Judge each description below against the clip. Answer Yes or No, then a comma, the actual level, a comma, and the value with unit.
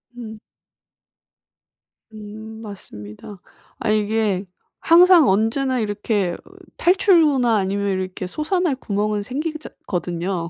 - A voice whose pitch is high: Yes, high, 215 Hz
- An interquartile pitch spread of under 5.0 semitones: No, wide, 5.5 semitones